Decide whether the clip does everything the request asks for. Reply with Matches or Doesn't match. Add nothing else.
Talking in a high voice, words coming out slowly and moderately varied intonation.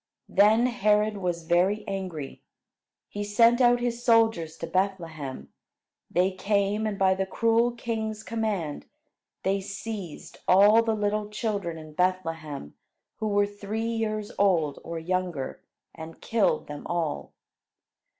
Matches